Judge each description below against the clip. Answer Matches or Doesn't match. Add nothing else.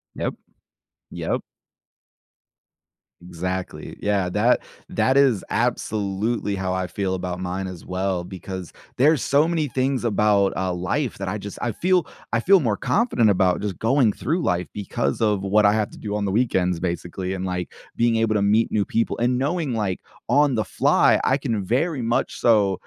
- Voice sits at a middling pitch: Doesn't match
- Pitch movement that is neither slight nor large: Matches